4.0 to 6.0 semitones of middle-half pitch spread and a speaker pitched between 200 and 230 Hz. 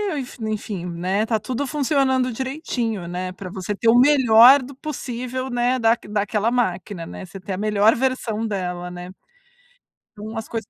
Yes: average, 4.6 semitones; high, 225 Hz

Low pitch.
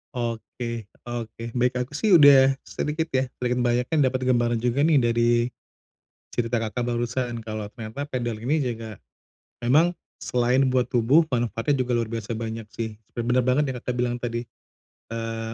Yes: low, 120 Hz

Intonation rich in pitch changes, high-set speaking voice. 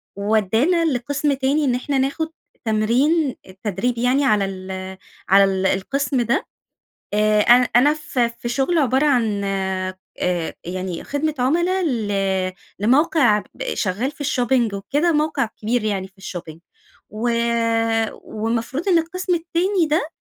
Yes: wide, 6.3 semitones; high, 245 Hz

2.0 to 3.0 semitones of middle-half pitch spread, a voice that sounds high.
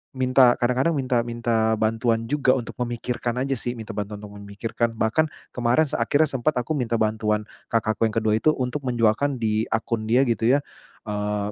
No: narrow, 2.6 semitones; low, 115 Hz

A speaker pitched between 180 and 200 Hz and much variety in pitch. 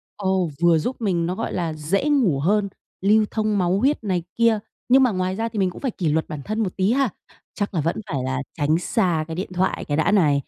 No: high, 190 Hz; average, 4.7 semitones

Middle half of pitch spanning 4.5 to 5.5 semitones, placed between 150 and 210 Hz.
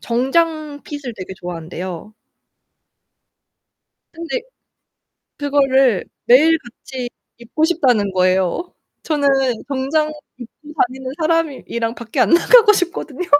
No: average, 5.2 semitones; very high, 270 Hz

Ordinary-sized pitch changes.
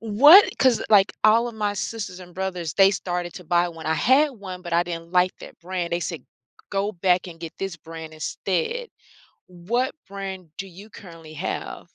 Yes: average, 3.1 semitones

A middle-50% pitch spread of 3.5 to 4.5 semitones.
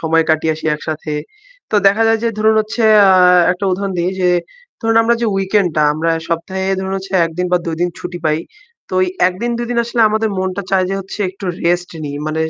Yes: average, 4.1 semitones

